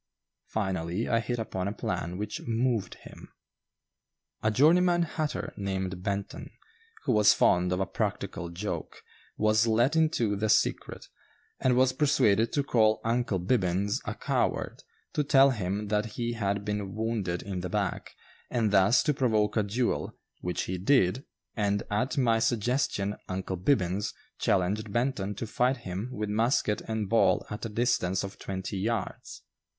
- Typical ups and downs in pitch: Yes, average, 3.7 semitones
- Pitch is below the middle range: Yes, low, 105 Hz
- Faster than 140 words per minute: Yes, average, 155 wpm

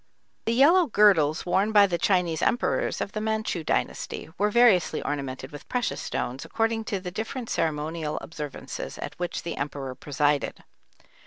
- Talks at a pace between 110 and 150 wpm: No, average, 160 wpm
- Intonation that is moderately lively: No, wide, 6.7 semitones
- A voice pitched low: No, medium, 180 Hz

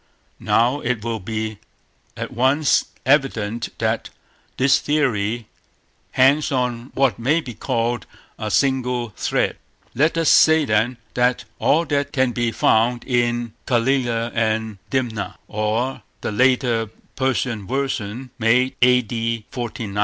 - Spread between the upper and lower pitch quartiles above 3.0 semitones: No, average, 2.7 semitones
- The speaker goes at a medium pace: No, slow, 120 wpm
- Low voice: Yes, low, 120 Hz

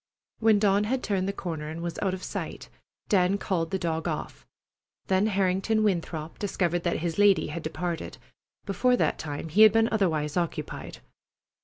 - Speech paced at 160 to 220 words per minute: Yes, average, 170 wpm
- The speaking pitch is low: No, medium, 185 Hz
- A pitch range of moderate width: Yes, average, 3.7 semitones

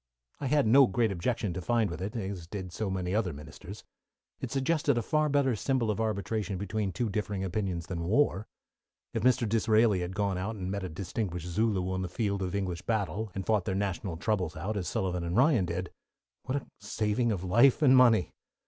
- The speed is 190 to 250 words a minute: Yes, fast, 205 wpm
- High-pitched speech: No, low, 100 Hz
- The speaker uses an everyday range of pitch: Yes, average, 3.9 semitones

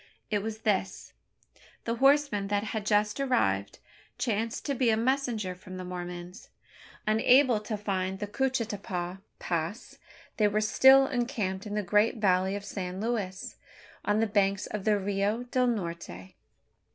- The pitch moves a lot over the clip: No, average, 3.4 semitones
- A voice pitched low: No, high, 210 Hz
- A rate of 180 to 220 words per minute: No, average, 150 wpm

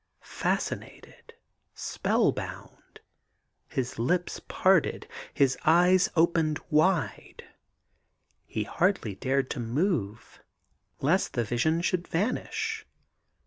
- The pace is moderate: No, slow, 90 wpm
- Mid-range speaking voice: Yes, medium, 160 Hz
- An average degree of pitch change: No, wide, 6.0 semitones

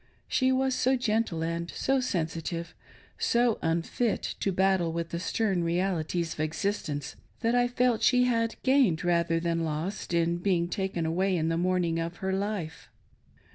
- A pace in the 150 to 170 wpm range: Yes, average, 160 wpm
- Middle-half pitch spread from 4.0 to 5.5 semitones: Yes, average, 5.1 semitones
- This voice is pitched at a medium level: Yes, medium, 180 Hz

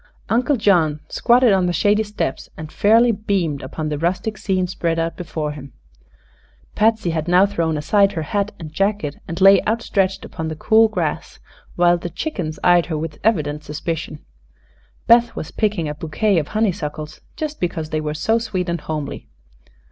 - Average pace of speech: Yes, average, 170 wpm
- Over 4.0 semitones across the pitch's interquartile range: Yes, average, 5.1 semitones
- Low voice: No, medium, 175 Hz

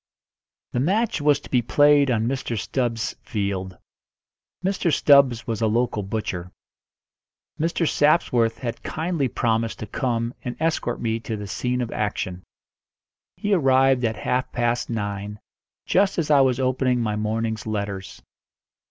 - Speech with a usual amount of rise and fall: Yes, average, 3.9 semitones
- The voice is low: Yes, low, 120 Hz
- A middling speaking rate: Yes, average, 145 wpm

